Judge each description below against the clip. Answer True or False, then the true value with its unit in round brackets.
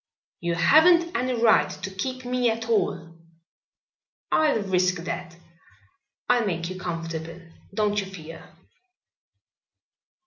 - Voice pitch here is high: True (195 Hz)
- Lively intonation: True (6.4 semitones)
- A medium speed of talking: False (110 wpm)